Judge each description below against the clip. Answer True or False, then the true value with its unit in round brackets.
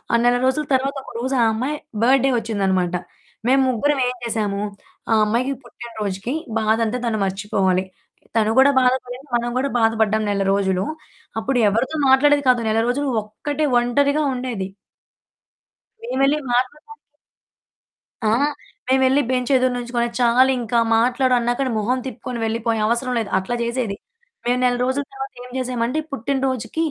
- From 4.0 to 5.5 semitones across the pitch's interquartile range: False (3.0 semitones)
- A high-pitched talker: True (245 Hz)